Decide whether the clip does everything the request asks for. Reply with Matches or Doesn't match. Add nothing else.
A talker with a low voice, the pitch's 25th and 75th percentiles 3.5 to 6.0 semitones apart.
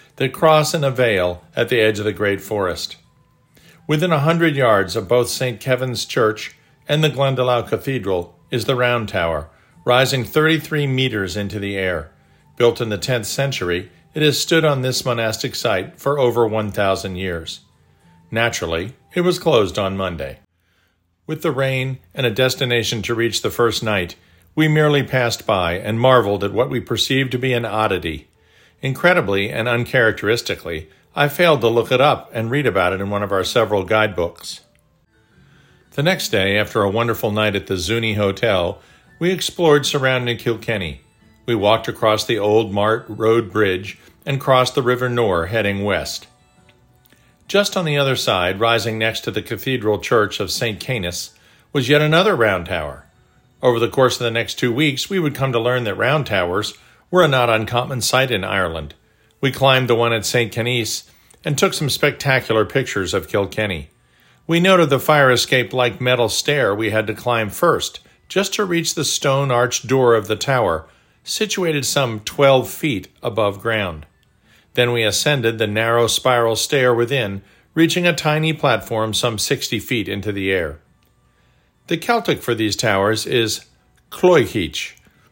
Matches